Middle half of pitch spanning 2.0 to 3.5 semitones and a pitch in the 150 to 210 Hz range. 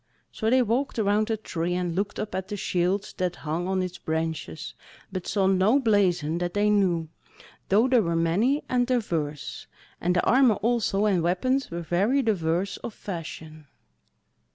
No: average, 4.2 semitones; high, 190 Hz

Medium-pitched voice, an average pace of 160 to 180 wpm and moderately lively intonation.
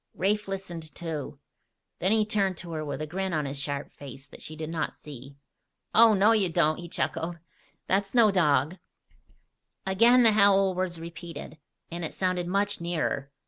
Yes: medium, 175 Hz; average, 175 wpm; average, 4.0 semitones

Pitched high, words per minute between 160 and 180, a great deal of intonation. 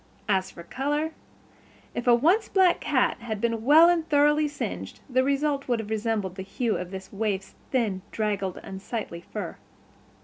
Yes: high, 235 Hz; average, 165 wpm; wide, 6.5 semitones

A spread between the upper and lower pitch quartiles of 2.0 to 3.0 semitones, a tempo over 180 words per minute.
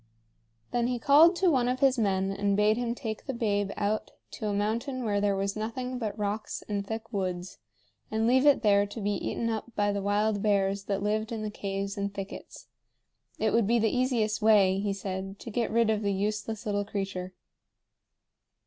Yes: narrow, 2.4 semitones; average, 200 wpm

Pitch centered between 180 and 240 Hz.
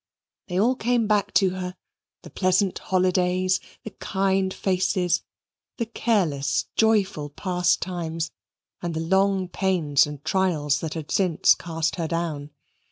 Yes: medium, 185 Hz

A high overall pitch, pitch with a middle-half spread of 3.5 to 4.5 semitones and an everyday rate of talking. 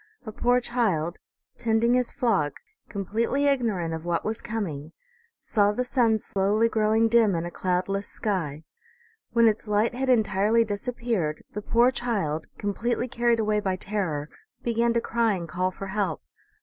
Yes: high, 215 Hz; average, 4.0 semitones; average, 160 wpm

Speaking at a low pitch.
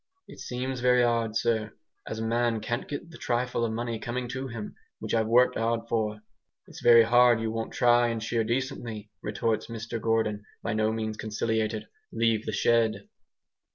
Yes: low, 115 Hz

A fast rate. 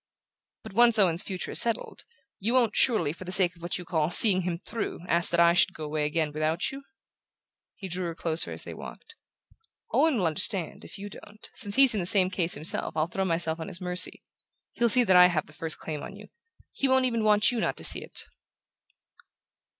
Yes: fast, 220 wpm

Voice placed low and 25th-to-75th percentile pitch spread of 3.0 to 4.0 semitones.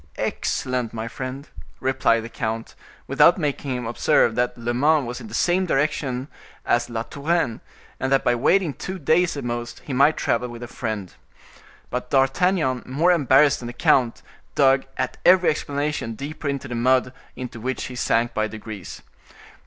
Yes: low, 130 Hz; average, 3.5 semitones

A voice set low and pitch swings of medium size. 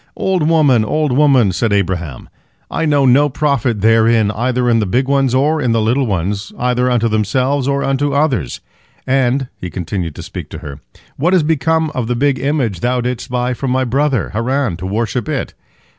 Yes: low, 125 Hz; average, 4.2 semitones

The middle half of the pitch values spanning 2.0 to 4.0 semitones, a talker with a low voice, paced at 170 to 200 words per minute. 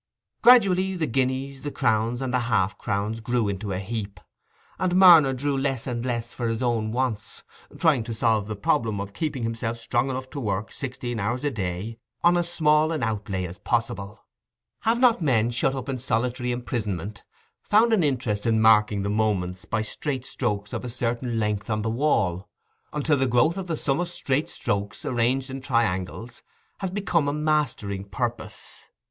No: average, 4.4 semitones; low, 120 Hz; average, 180 wpm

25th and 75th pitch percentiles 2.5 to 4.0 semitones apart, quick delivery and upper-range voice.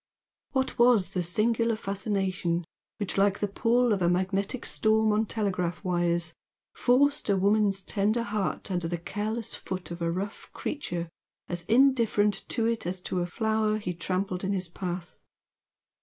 No: average, 3.4 semitones; average, 155 wpm; high, 200 Hz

